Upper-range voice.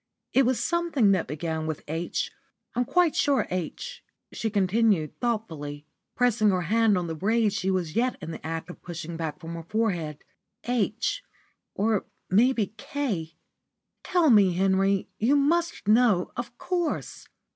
Yes: high, 205 Hz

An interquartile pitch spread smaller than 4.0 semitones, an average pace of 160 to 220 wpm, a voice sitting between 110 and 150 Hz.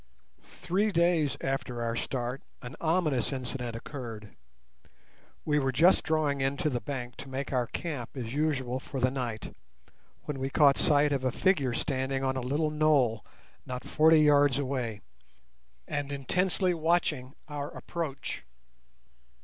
No: average, 3.2 semitones; average, 145 wpm; medium, 140 Hz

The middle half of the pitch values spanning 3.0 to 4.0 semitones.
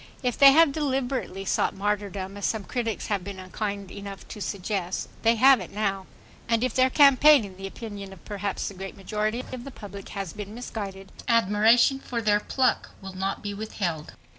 Yes: average, 3.5 semitones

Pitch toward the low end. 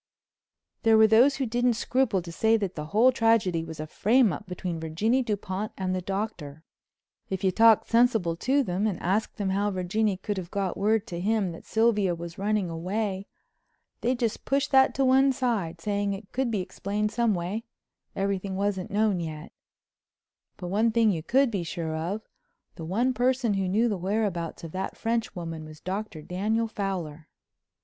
No: high, 200 Hz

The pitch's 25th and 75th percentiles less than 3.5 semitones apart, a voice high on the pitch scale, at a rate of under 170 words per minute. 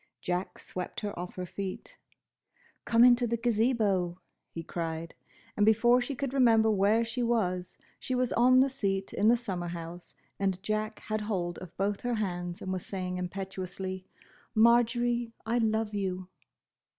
No: average, 4.3 semitones; high, 205 Hz; average, 160 wpm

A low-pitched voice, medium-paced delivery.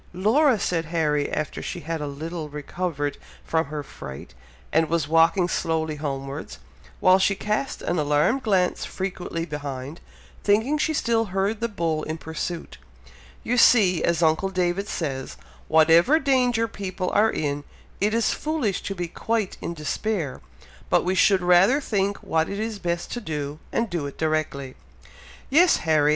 No: medium, 175 Hz; average, 160 wpm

